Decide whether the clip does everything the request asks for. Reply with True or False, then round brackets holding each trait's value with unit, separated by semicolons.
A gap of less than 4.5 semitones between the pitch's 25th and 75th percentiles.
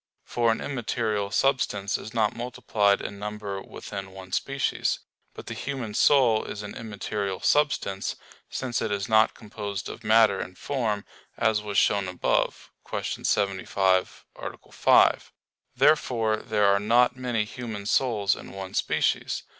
True (2.9 semitones)